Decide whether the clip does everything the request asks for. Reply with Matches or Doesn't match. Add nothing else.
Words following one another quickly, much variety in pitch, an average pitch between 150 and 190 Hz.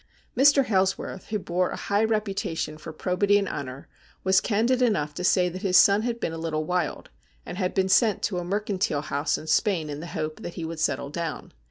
Doesn't match